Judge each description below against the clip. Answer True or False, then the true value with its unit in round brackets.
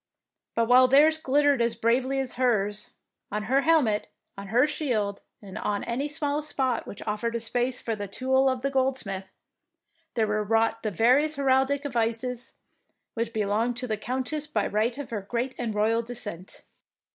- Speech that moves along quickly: False (180 wpm)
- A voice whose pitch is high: True (240 Hz)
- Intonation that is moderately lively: True (3.7 semitones)